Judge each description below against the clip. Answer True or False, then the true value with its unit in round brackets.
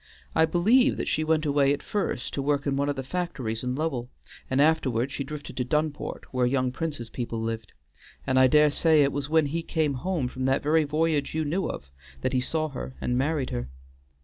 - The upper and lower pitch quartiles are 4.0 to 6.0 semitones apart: False (3.5 semitones)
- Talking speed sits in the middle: False (220 wpm)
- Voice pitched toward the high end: False (145 Hz)